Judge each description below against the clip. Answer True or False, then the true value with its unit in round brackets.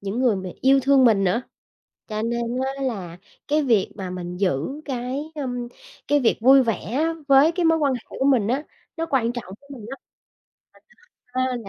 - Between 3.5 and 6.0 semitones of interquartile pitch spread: True (4.4 semitones)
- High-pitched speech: True (250 Hz)